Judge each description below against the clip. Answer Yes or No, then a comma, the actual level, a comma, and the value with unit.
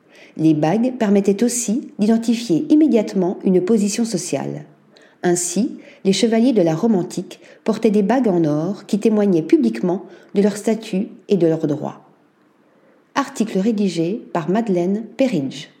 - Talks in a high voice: Yes, high, 205 Hz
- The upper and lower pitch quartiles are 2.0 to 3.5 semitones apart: No, average, 4.5 semitones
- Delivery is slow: Yes, slow, 135 wpm